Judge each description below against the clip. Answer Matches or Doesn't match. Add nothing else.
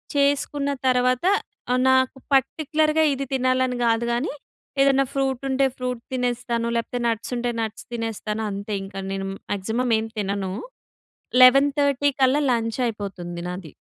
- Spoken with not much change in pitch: Doesn't match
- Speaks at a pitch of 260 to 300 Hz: Doesn't match